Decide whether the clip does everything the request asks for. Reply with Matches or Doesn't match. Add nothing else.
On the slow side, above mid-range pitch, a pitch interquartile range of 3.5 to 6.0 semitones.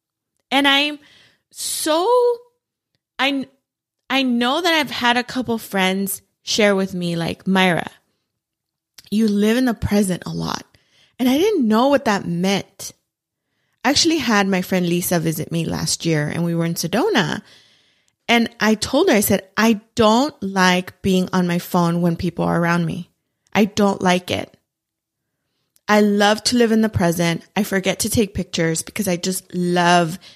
Doesn't match